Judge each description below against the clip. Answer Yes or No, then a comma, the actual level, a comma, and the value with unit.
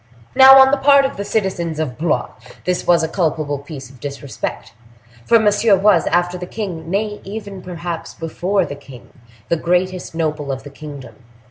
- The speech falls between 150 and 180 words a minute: Yes, average, 165 wpm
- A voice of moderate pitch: Yes, medium, 175 Hz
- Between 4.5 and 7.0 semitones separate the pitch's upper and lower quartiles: Yes, wide, 5.6 semitones